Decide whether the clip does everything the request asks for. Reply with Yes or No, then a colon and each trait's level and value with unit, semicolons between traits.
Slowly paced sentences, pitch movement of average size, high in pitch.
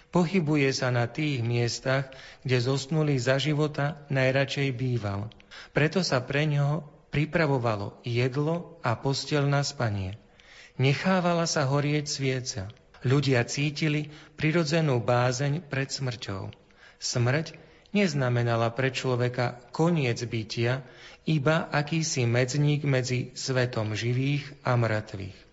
No: slow, 105 wpm; average, 3.5 semitones; low, 135 Hz